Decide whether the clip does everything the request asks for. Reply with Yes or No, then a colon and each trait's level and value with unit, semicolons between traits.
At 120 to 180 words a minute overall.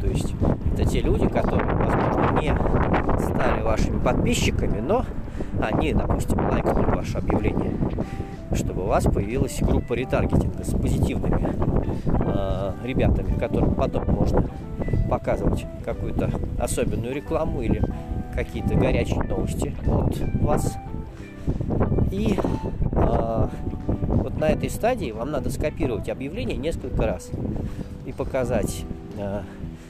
No: slow, 110 wpm